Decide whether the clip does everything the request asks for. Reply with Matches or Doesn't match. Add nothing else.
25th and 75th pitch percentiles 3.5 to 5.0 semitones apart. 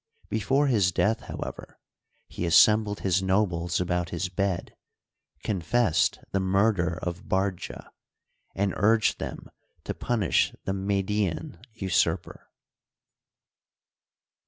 Doesn't match